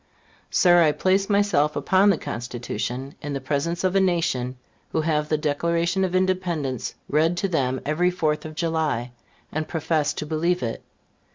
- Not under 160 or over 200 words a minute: Yes, average, 165 wpm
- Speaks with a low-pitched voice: No, medium, 160 Hz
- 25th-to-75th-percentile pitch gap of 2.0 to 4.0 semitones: Yes, average, 3.6 semitones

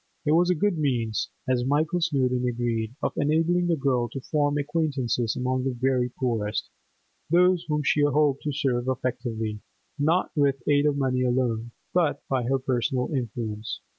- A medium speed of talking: Yes, average, 160 wpm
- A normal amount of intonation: Yes, average, 3.5 semitones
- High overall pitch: No, low, 135 Hz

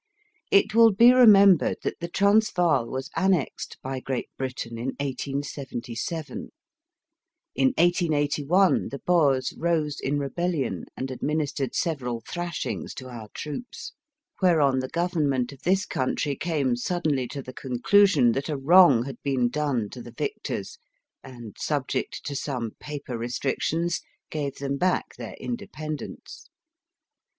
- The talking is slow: Yes, slow, 130 wpm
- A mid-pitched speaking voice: Yes, medium, 145 Hz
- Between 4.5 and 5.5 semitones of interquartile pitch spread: Yes, average, 5.1 semitones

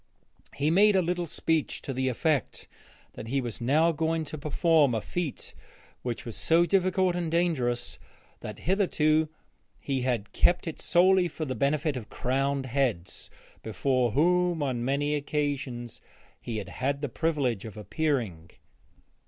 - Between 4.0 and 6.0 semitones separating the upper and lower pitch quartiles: Yes, average, 4.9 semitones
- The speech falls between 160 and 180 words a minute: No, average, 150 wpm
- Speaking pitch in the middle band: Yes, medium, 145 Hz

